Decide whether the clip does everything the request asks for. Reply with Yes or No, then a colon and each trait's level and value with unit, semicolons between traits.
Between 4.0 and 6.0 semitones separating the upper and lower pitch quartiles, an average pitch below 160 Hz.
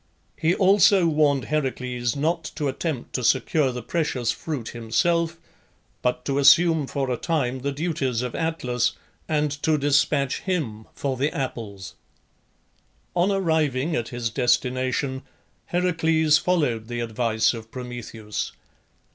Yes: average, 4.6 semitones; medium, 140 Hz